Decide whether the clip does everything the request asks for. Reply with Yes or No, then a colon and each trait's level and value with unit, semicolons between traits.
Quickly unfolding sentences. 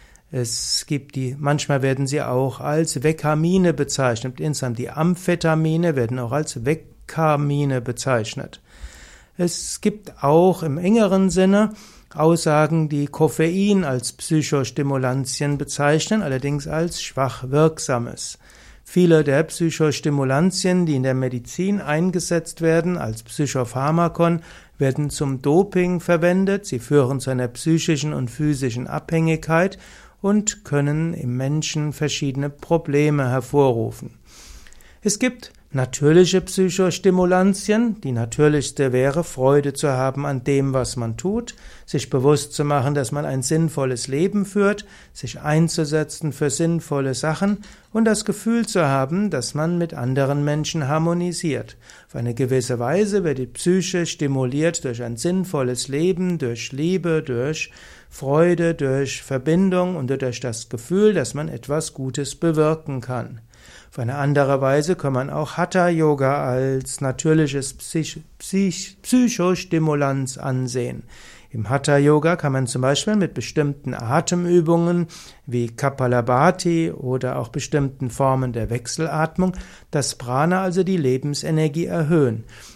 No: slow, 125 wpm